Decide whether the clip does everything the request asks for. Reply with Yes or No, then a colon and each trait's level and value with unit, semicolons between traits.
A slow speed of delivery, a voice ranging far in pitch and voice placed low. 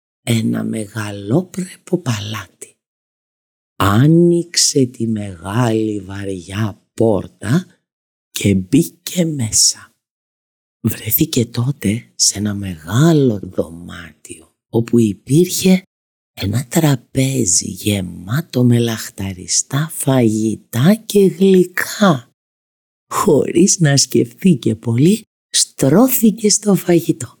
Yes: slow, 75 wpm; wide, 8.4 semitones; low, 120 Hz